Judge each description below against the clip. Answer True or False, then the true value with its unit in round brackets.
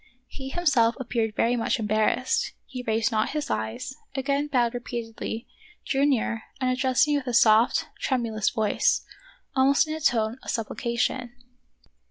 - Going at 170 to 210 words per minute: False (155 wpm)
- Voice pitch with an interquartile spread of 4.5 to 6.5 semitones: False (3.0 semitones)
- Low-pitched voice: False (245 Hz)